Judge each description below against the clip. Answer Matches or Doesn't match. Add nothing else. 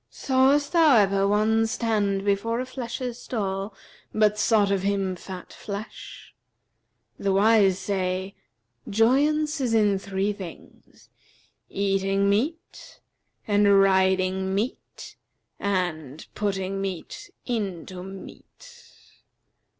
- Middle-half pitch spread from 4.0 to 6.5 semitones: Doesn't match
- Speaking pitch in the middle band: Doesn't match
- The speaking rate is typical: Doesn't match